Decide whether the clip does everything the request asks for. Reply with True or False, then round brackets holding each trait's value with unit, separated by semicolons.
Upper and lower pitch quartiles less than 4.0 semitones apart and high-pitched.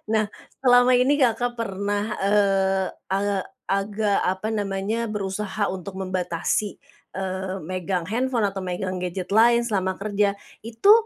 True (2.6 semitones; 200 Hz)